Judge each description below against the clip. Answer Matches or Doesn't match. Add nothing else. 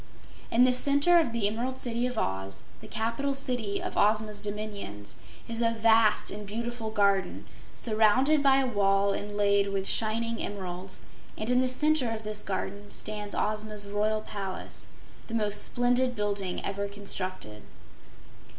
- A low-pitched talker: Doesn't match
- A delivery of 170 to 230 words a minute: Doesn't match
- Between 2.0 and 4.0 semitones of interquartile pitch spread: Matches